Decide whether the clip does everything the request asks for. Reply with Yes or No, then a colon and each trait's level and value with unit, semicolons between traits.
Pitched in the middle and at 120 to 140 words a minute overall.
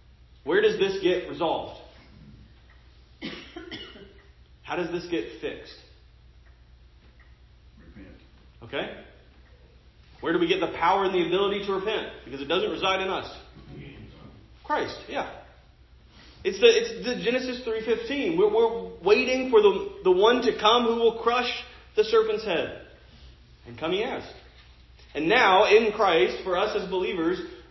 No: high, 200 Hz; slow, 135 wpm